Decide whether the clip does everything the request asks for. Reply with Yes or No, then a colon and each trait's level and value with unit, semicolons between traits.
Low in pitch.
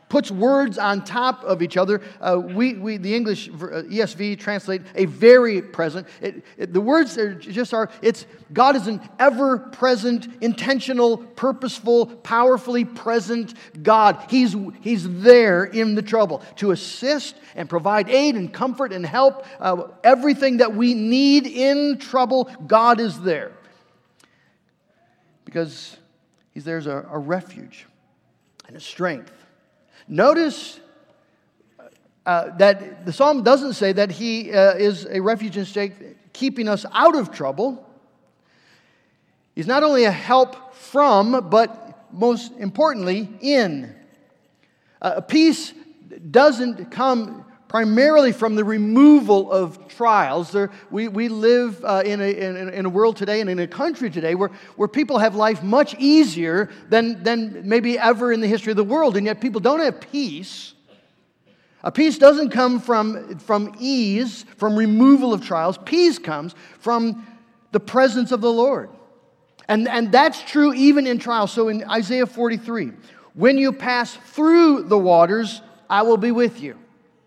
No: high, 230 Hz